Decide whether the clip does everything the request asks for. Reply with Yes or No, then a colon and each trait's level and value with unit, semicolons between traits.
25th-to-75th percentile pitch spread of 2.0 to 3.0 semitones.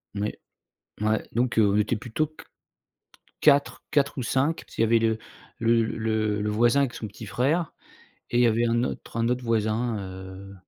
Yes: narrow, 2.4 semitones